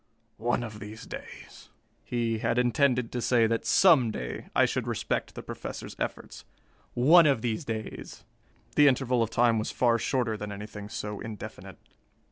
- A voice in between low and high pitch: No, low, 115 Hz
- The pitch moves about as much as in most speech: No, narrow, 2.3 semitones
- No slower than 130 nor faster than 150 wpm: No, average, 160 wpm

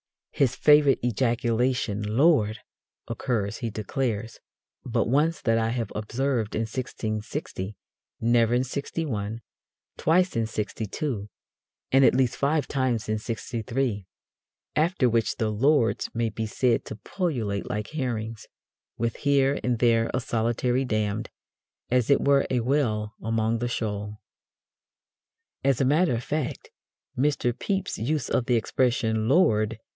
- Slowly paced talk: Yes, slow, 130 wpm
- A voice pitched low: Yes, low, 120 Hz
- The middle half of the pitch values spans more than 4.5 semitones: No, average, 3.5 semitones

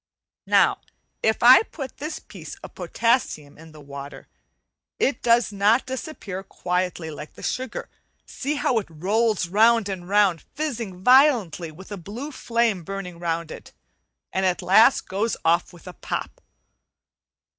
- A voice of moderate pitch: No, high, 200 Hz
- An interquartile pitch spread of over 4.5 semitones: Yes, average, 5.2 semitones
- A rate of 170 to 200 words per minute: No, average, 145 wpm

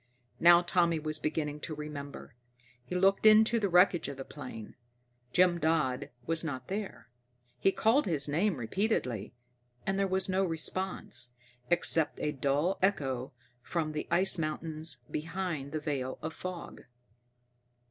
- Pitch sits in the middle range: Yes, medium, 160 Hz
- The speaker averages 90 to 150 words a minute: Yes, average, 140 wpm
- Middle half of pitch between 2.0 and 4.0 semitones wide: No, average, 4.4 semitones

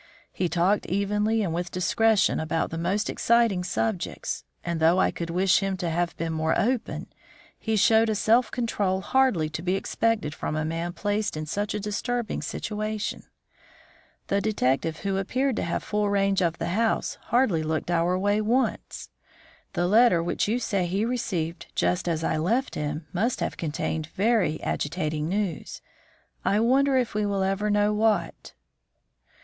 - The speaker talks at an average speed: Yes, average, 165 wpm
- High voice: Yes, high, 195 Hz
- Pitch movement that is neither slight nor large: Yes, average, 4.5 semitones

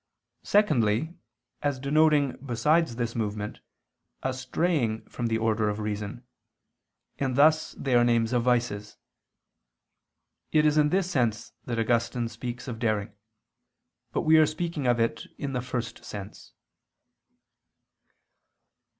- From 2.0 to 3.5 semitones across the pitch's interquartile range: No, average, 4.8 semitones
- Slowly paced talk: Yes, slow, 125 wpm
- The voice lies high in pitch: No, low, 120 Hz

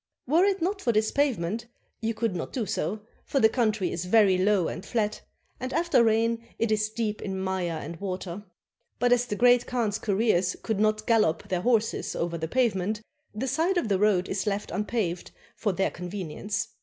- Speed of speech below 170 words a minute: No, average, 195 wpm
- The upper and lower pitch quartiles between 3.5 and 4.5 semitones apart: Yes, average, 3.8 semitones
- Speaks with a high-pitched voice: Yes, high, 215 Hz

